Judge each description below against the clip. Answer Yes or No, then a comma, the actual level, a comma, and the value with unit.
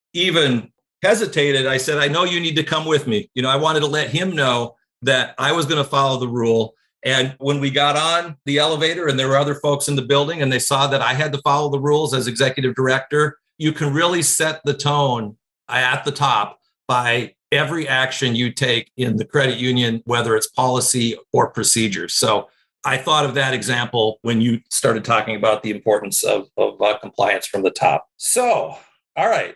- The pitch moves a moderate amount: Yes, average, 3.3 semitones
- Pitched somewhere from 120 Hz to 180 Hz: Yes, medium, 140 Hz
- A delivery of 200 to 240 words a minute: Yes, fast, 205 wpm